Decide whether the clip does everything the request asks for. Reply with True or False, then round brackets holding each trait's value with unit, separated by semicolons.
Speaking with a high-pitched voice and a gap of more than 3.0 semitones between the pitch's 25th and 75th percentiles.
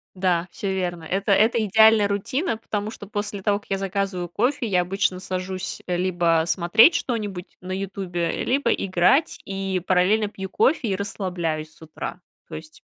False (195 Hz; 2.7 semitones)